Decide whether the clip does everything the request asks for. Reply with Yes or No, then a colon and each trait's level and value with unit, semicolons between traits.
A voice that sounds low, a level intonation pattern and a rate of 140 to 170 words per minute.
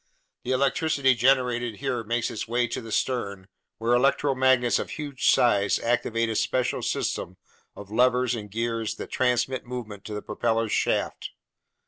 Yes: low, 120 Hz; narrow, 2.3 semitones; average, 150 wpm